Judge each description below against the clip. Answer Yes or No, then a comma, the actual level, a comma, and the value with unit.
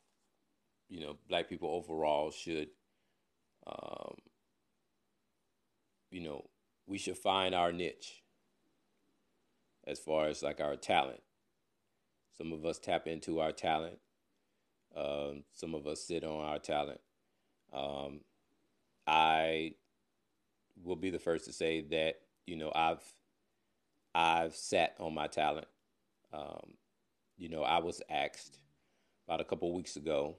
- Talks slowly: Yes, slow, 125 wpm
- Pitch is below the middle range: Yes, very low, 80 Hz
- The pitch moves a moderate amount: No, narrow, 2.3 semitones